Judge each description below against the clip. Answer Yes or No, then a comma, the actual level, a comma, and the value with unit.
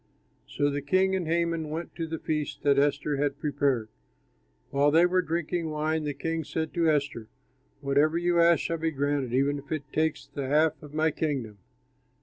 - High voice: No, medium, 150 Hz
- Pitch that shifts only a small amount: Yes, narrow, 2.3 semitones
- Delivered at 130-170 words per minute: No, average, 185 wpm